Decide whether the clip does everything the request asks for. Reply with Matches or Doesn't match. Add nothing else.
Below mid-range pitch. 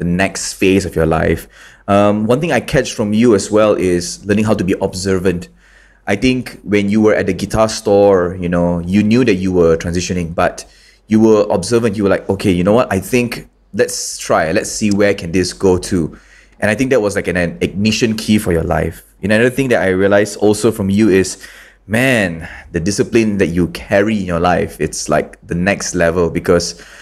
Matches